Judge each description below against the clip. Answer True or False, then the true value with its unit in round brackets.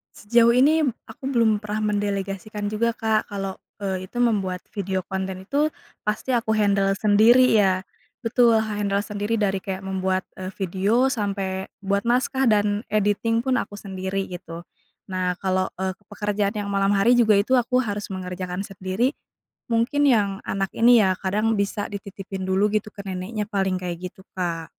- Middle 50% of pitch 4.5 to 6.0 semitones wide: False (2.7 semitones)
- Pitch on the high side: True (205 Hz)